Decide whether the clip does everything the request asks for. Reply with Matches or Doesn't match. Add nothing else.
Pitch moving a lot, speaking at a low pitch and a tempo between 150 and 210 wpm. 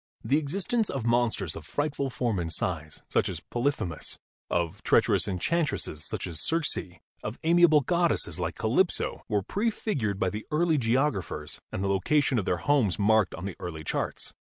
Matches